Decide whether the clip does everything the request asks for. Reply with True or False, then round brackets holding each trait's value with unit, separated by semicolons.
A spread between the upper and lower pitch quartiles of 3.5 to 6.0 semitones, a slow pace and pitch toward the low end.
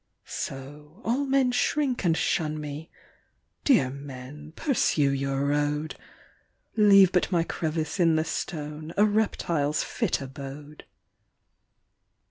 False (5.0 semitones; 110 wpm; 155 Hz)